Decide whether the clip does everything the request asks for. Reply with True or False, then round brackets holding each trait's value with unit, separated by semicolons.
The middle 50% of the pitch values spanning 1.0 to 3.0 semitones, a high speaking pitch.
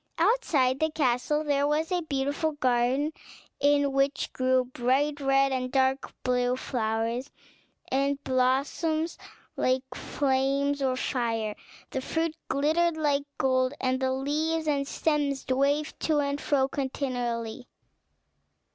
True (2.4 semitones; 275 Hz)